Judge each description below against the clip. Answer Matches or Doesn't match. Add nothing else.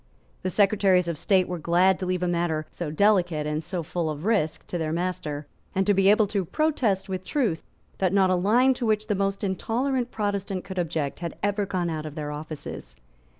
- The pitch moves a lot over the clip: Doesn't match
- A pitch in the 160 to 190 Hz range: Matches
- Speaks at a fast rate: Matches